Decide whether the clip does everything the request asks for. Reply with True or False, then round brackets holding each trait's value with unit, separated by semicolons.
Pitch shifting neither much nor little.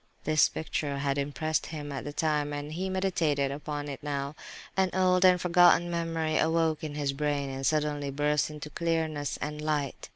False (2.0 semitones)